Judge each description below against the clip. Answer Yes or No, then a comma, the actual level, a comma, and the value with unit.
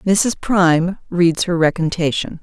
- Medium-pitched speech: Yes, medium, 175 Hz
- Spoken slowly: Yes, slow, 125 wpm